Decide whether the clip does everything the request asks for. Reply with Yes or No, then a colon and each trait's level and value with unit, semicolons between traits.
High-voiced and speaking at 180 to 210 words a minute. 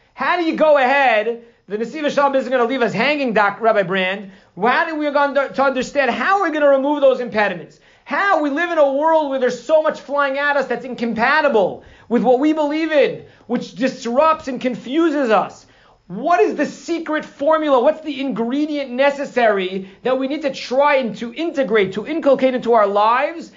Yes: very high, 270 Hz; average, 195 wpm